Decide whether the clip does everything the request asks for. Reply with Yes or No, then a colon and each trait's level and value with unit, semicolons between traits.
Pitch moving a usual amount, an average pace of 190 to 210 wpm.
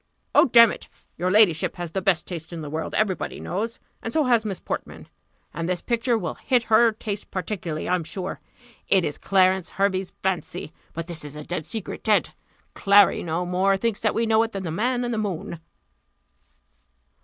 Yes: average, 4.2 semitones; average, 195 wpm